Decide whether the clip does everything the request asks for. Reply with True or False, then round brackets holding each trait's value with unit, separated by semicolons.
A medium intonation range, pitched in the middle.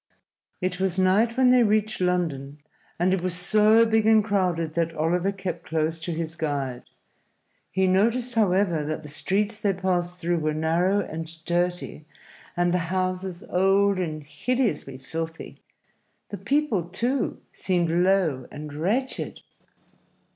True (3.7 semitones; 180 Hz)